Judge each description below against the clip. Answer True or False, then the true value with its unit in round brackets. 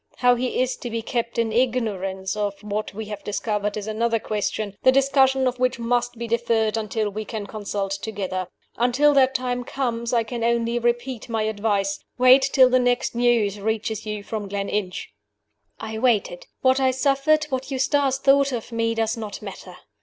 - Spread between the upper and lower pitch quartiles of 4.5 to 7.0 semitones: False (3.2 semitones)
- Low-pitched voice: False (230 Hz)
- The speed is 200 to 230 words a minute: False (180 wpm)